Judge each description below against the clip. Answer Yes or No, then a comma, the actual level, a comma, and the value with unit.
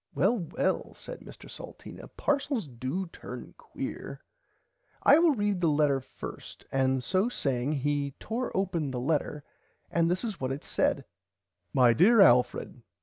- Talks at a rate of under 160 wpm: Yes, average, 145 wpm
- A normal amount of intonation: No, wide, 7.5 semitones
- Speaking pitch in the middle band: Yes, medium, 155 Hz